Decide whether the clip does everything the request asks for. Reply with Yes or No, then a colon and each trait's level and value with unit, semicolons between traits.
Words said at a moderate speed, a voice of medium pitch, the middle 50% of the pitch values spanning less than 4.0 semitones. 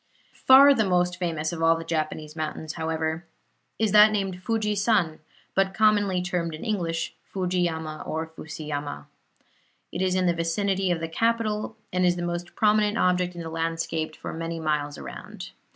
Yes: average, 170 wpm; medium, 175 Hz; average, 3.4 semitones